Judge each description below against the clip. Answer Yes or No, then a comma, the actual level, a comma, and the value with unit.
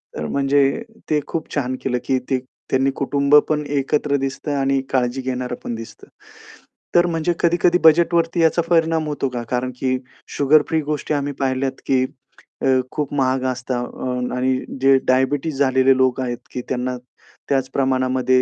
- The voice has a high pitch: No, low, 135 Hz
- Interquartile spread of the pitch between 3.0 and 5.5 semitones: No, narrow, 2.6 semitones